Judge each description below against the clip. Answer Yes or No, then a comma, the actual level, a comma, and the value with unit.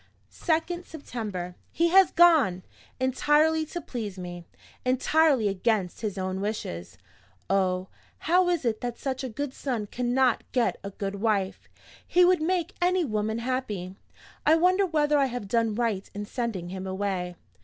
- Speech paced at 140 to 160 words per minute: Yes, average, 155 wpm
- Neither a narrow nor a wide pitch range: No, wide, 7.9 semitones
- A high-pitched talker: Yes, high, 240 Hz